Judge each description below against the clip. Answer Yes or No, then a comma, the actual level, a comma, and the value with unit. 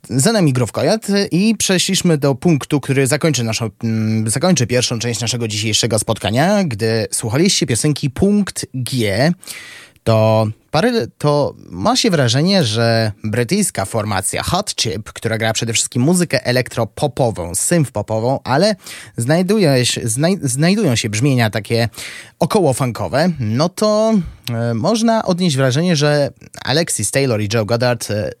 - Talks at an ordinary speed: Yes, average, 130 wpm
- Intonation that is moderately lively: No, wide, 6.8 semitones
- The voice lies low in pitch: Yes, low, 130 Hz